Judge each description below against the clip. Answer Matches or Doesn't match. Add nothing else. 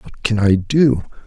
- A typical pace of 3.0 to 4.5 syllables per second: Matches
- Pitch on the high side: Doesn't match